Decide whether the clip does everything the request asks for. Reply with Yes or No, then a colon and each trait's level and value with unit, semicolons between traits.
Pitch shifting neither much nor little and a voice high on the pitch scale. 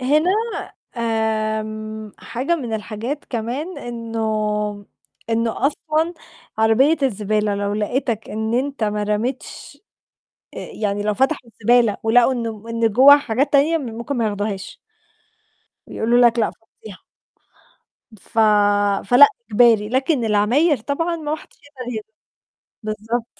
Yes: average, 3.7 semitones; high, 230 Hz